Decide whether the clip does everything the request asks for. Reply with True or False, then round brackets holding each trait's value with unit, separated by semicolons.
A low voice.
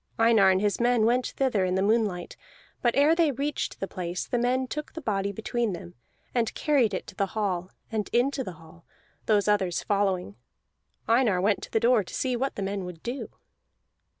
False (215 Hz)